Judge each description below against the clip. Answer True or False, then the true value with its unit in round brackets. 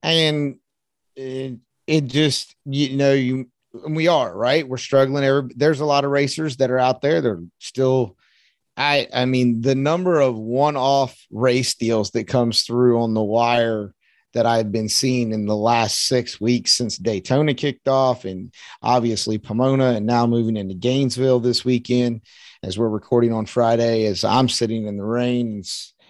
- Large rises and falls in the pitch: False (2.7 semitones)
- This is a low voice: True (125 Hz)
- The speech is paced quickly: False (170 wpm)